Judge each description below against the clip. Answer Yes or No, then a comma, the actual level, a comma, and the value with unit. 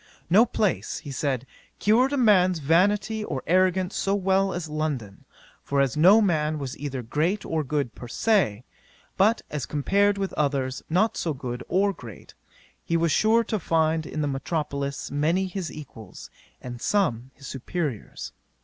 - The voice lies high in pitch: No, medium, 160 Hz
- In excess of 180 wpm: No, average, 160 wpm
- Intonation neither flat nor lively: No, wide, 5.8 semitones